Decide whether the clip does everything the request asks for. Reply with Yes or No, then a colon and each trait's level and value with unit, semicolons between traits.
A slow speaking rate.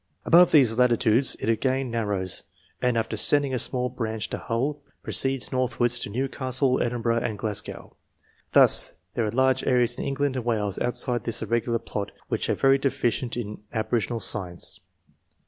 No: average, 165 wpm